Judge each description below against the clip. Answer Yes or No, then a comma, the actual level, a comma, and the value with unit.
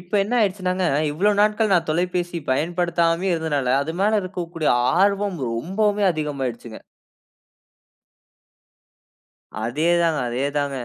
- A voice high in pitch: No, medium, 175 Hz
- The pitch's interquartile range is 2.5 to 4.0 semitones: No, average, 4.5 semitones